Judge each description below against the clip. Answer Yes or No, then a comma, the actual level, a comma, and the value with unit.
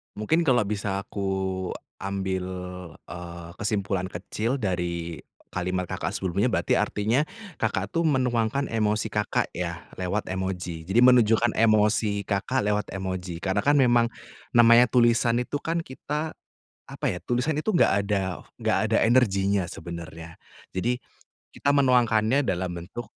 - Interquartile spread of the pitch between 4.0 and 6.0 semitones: Yes, average, 4.4 semitones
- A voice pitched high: No, low, 105 Hz